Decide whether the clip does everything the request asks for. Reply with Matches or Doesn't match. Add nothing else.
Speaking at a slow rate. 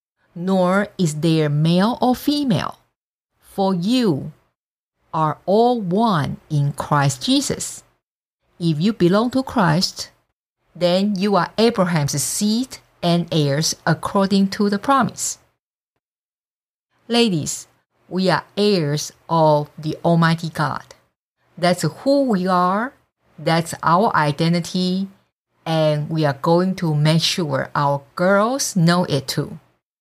Matches